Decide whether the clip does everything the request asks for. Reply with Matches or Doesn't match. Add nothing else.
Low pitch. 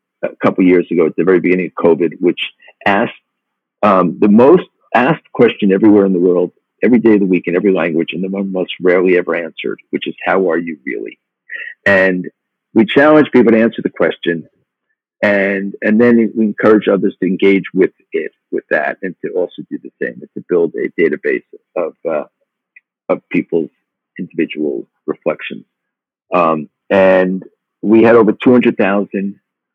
Matches